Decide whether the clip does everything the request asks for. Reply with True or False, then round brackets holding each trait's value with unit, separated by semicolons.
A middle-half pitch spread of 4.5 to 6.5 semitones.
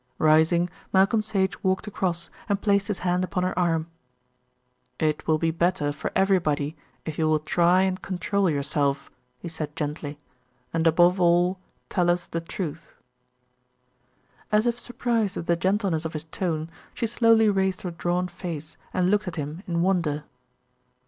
False (3.2 semitones)